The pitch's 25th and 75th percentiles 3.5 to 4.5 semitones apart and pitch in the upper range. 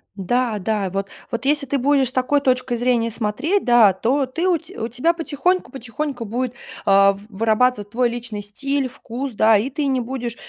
Yes: average, 3.8 semitones; high, 245 Hz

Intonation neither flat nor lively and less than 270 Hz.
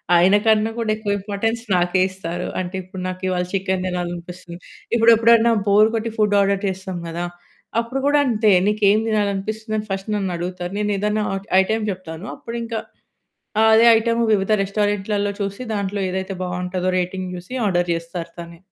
Yes: average, 3.0 semitones; high, 195 Hz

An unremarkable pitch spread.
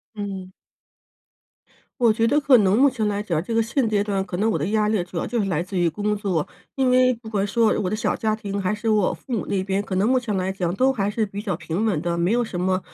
Yes: average, 3.0 semitones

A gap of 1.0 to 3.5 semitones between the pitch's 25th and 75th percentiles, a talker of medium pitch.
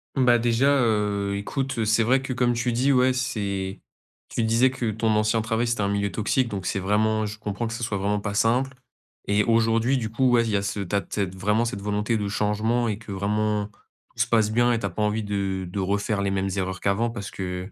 No: narrow, 2.6 semitones; low, 110 Hz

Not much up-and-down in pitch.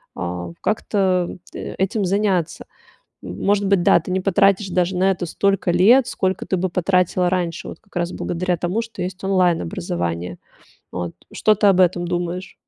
Yes: narrow, 2.2 semitones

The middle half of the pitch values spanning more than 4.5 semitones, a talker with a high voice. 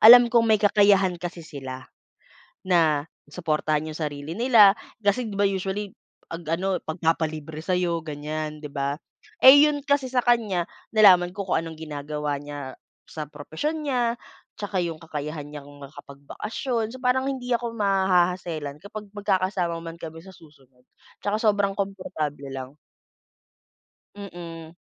No: average, 5.2 semitones; medium, 175 Hz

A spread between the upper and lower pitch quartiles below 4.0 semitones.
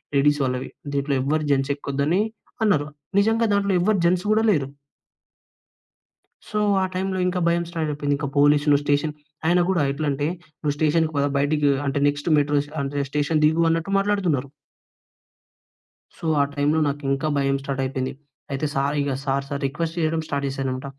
Yes: average, 3.1 semitones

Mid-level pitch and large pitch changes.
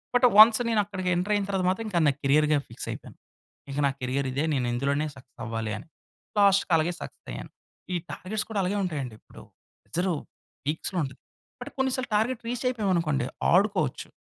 Yes: medium, 175 Hz; wide, 6.8 semitones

